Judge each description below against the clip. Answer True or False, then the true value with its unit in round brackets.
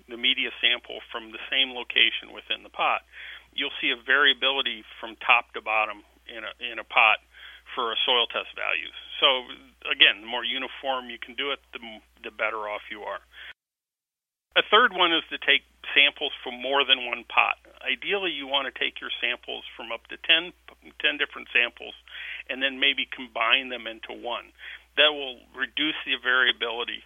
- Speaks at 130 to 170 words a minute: False (180 wpm)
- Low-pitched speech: True (130 Hz)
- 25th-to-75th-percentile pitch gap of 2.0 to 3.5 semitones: True (2.9 semitones)